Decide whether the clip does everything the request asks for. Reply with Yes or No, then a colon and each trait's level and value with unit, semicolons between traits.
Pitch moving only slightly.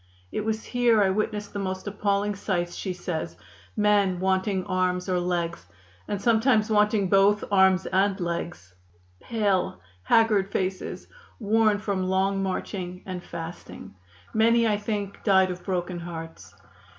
Yes: narrow, 2.3 semitones